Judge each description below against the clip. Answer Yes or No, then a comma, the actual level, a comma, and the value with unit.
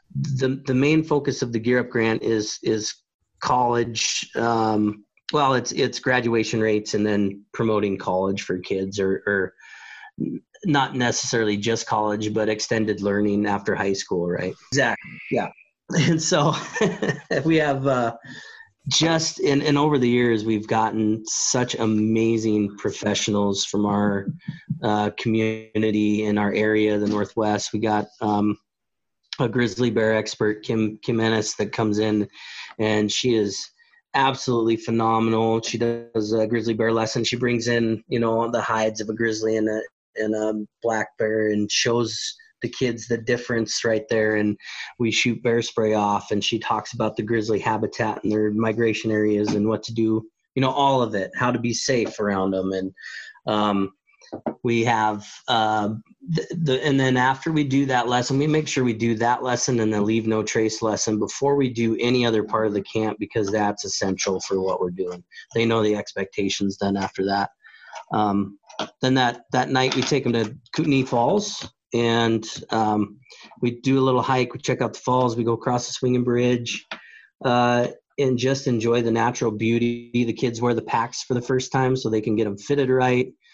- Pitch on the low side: Yes, low, 115 Hz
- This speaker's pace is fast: No, average, 175 wpm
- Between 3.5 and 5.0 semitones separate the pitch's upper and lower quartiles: No, average, 2.9 semitones